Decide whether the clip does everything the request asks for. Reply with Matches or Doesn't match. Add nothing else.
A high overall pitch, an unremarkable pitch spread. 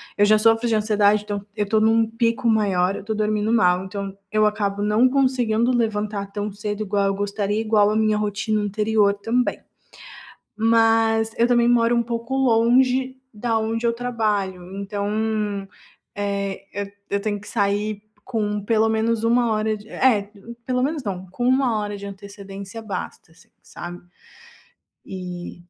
Doesn't match